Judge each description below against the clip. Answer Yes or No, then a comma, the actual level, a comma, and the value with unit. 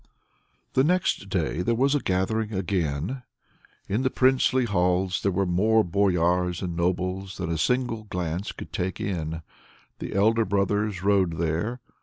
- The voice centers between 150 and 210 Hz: No, very low, 95 Hz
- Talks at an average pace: Yes, average, 150 wpm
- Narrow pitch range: No, average, 3.8 semitones